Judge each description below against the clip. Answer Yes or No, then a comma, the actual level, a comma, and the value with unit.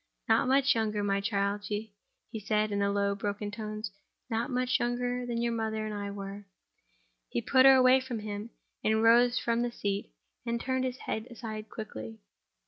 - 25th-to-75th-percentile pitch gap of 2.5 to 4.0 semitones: Yes, average, 2.9 semitones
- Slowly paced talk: No, average, 170 wpm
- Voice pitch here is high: Yes, high, 220 Hz